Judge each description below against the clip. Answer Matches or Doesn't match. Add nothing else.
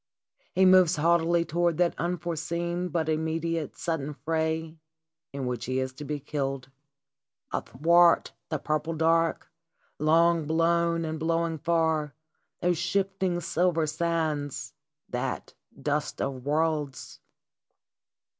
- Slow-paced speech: Matches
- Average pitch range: Doesn't match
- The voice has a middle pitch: Matches